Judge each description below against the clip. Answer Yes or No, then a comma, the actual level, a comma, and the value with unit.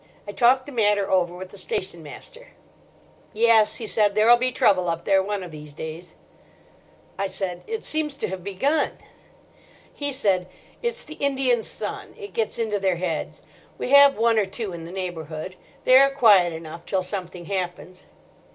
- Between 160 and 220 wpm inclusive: Yes, average, 180 wpm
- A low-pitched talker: No, high, 200 Hz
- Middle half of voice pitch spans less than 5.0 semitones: No, average, 5.3 semitones